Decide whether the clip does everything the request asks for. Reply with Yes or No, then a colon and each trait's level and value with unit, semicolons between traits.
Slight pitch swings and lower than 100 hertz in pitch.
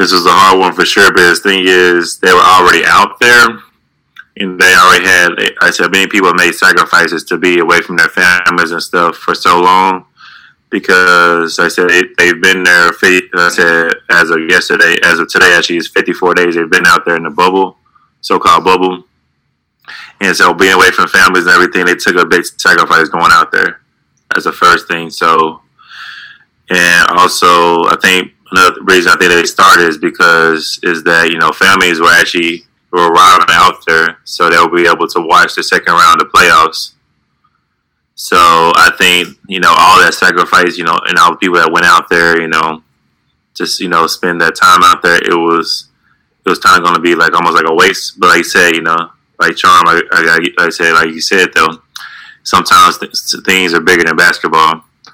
Yes: narrow, 1.4 semitones; very low, 85 Hz